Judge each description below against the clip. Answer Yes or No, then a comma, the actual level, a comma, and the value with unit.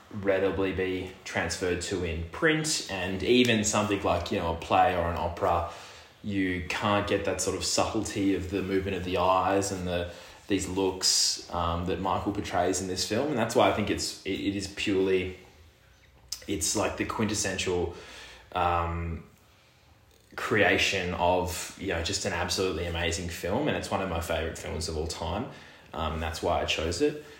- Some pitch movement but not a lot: No, narrow, 2.3 semitones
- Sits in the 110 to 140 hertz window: No, very low, 95 Hz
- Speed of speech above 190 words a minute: No, average, 175 wpm